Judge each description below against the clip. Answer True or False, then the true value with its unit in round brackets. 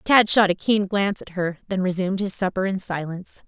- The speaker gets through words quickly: True (225 wpm)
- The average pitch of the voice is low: False (190 Hz)